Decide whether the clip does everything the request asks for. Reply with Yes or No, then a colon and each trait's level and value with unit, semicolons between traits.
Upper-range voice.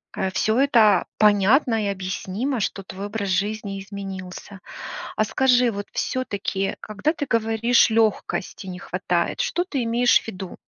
Yes: high, 210 Hz